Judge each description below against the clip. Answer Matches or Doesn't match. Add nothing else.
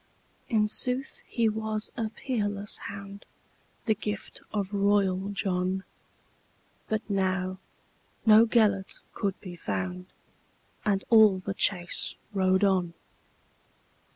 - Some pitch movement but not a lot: Doesn't match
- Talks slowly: Matches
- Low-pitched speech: Doesn't match